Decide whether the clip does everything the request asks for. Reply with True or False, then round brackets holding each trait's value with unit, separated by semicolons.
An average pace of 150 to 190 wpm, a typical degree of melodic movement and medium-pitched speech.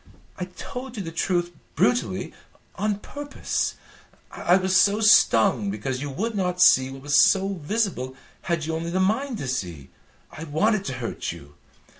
False (165 wpm; 7.3 semitones; 175 Hz)